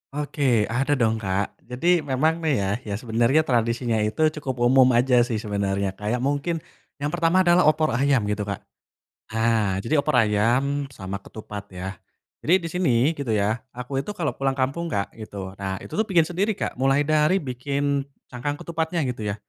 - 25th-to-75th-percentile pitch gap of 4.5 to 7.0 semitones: Yes, average, 5.3 semitones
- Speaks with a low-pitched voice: Yes, low, 130 Hz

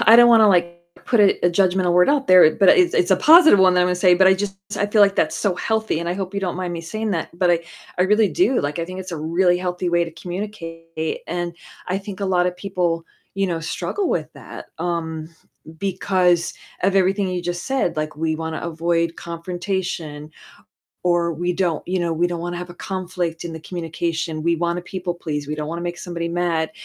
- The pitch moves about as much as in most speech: No, narrow, 2.1 semitones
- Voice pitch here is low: No, medium, 175 Hz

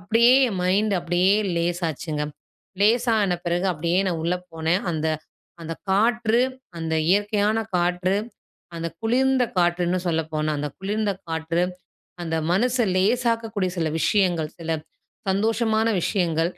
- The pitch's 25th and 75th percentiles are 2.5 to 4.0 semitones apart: No, average, 4.6 semitones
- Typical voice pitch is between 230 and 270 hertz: No, medium, 185 Hz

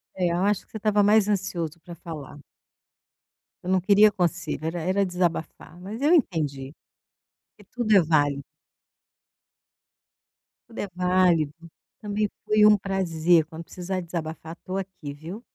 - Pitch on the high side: No, medium, 180 Hz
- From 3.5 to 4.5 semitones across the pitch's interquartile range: Yes, average, 3.9 semitones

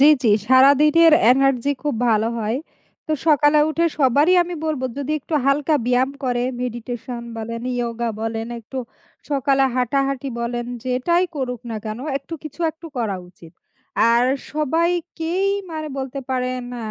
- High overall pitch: Yes, very high, 265 Hz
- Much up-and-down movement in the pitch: No, average, 4.0 semitones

